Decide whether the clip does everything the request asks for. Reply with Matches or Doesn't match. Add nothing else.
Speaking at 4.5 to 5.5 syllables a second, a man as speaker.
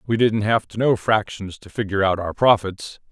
Matches